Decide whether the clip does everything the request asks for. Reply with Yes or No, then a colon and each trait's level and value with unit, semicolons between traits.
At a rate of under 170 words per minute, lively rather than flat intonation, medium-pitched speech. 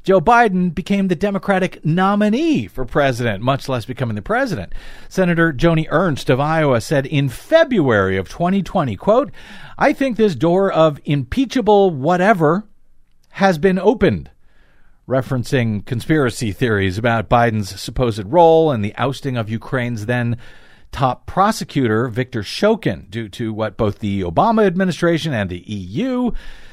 Yes: slow, 135 wpm; wide, 8.5 semitones; medium, 145 Hz